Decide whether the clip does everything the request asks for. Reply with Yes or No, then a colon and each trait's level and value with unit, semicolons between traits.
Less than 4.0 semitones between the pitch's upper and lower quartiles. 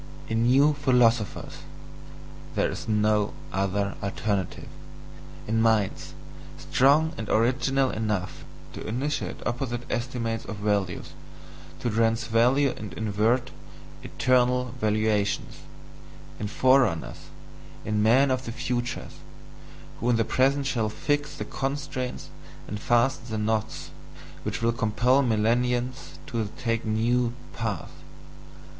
Yes: average, 3.0 semitones